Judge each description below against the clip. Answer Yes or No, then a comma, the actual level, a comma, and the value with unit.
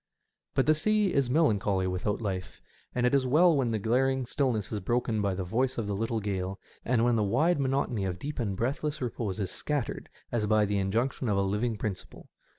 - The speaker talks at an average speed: No, fast, 210 wpm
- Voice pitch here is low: Yes, low, 115 Hz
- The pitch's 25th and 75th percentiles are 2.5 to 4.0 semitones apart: No, average, 4.8 semitones